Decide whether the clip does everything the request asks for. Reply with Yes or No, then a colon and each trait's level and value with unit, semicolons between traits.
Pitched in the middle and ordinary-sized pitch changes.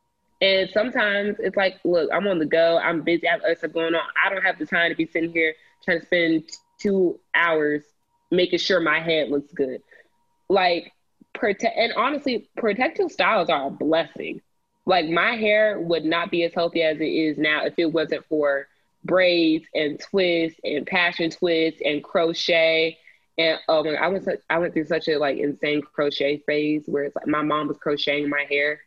Yes: medium, 165 Hz; average, 3.2 semitones